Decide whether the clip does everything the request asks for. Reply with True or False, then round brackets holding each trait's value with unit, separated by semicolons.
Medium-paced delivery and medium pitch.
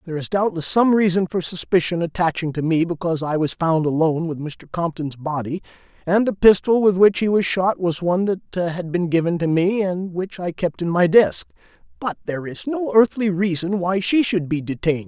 False (210 wpm; 170 Hz)